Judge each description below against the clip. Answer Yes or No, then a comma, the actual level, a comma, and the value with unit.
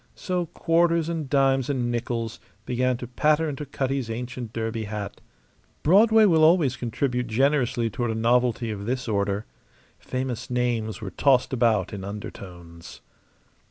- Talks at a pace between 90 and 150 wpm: Yes, average, 140 wpm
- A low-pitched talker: Yes, low, 125 Hz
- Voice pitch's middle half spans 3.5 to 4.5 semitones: Yes, average, 3.8 semitones